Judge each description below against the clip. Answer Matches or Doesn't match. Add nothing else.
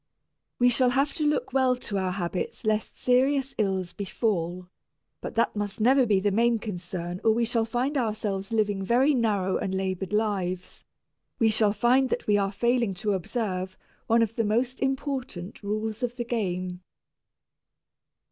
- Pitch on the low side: Doesn't match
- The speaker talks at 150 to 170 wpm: Matches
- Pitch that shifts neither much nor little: Matches